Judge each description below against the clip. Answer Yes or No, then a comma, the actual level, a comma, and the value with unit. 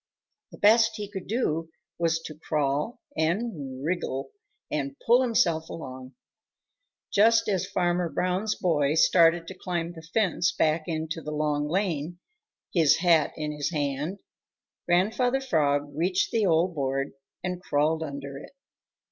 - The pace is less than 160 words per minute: Yes, average, 140 wpm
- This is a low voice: No, medium, 165 Hz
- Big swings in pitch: No, average, 3.8 semitones